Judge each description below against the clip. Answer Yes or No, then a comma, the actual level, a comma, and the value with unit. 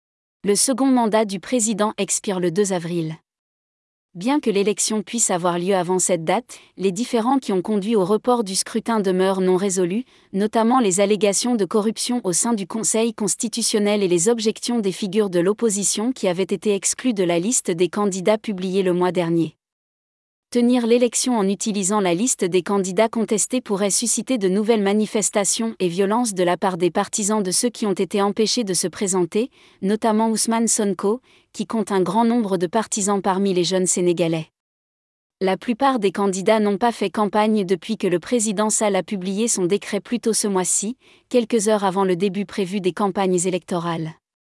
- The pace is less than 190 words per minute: Yes, average, 180 wpm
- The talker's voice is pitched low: No, high, 205 Hz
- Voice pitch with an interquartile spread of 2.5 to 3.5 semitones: Yes, average, 3.2 semitones